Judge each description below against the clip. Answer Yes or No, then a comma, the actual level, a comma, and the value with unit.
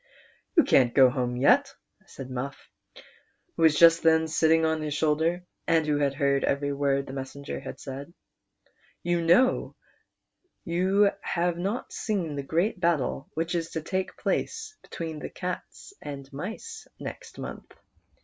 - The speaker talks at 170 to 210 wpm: No, average, 155 wpm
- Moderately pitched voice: Yes, medium, 160 Hz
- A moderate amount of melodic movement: Yes, average, 4.1 semitones